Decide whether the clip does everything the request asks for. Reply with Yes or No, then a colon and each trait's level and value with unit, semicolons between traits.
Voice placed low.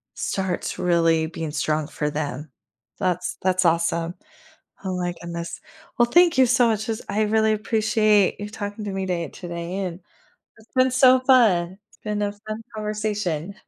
No: high, 195 Hz